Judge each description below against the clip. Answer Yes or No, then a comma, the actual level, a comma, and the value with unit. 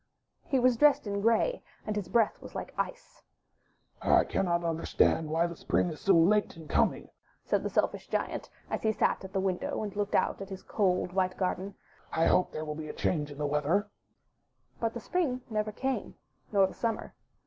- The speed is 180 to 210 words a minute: Yes, average, 200 wpm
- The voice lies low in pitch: No, high, 195 Hz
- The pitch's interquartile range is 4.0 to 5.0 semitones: Yes, average, 4.3 semitones